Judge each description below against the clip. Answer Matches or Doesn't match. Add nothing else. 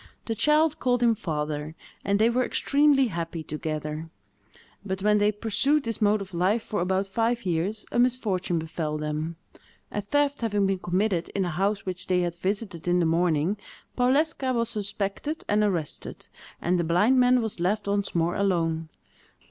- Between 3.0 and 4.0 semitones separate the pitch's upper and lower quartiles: Doesn't match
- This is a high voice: Matches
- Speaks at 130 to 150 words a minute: Doesn't match